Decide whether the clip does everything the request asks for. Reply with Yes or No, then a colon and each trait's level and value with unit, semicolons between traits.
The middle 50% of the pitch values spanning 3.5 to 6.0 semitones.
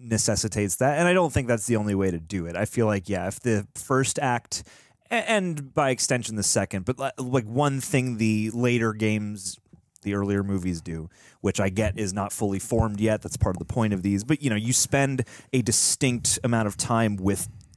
Yes: average, 4.2 semitones